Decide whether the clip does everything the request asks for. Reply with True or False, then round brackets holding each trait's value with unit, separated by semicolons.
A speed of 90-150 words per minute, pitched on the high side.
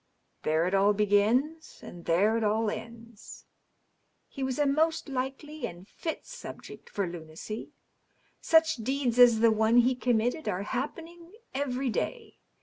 True (145 wpm; 235 Hz)